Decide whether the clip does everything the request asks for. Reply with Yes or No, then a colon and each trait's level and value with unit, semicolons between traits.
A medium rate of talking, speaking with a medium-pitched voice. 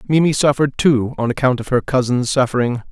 No: average, 185 wpm; low, 130 Hz